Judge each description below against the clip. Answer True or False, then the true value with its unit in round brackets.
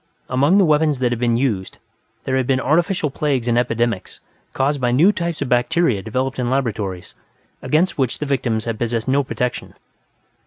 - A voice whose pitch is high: False (130 Hz)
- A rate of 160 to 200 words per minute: True (180 wpm)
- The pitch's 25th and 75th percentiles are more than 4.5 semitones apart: False (3.7 semitones)